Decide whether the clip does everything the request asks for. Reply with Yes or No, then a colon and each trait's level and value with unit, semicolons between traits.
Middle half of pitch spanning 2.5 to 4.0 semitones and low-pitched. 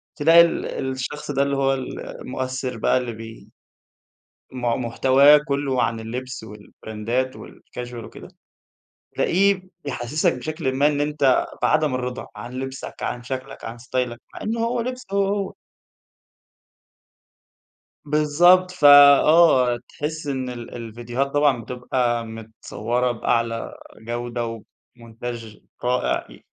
Yes: average, 3.6 semitones; low, 130 Hz